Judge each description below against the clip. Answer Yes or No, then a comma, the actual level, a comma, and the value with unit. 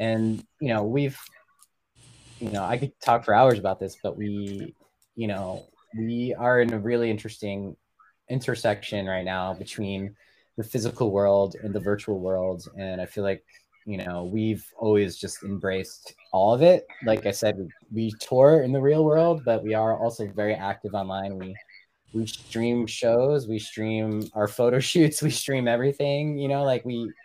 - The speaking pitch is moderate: No, low, 110 Hz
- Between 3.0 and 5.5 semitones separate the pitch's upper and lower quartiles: Yes, average, 3.4 semitones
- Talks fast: No, average, 175 wpm